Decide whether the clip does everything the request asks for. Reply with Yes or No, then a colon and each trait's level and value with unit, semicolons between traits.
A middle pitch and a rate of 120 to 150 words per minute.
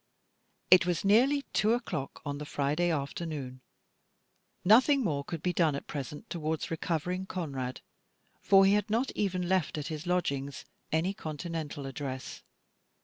Yes: medium, 165 Hz; average, 145 wpm